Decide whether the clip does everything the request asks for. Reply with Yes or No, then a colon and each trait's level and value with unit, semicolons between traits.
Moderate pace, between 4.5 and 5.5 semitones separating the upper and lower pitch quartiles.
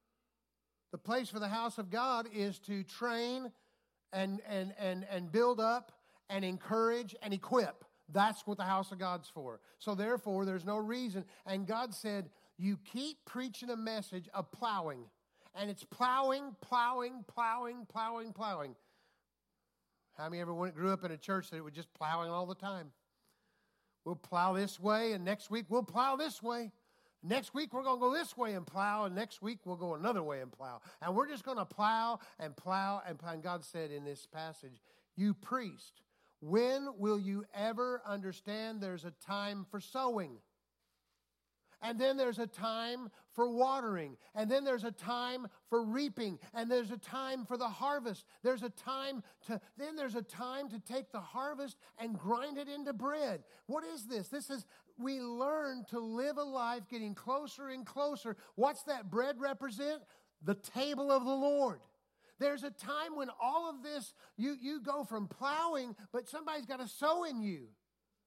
Yes: average, 180 wpm; average, 5.0 semitones